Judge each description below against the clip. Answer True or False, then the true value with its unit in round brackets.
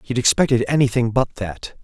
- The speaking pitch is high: False (120 Hz)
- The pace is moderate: True (195 wpm)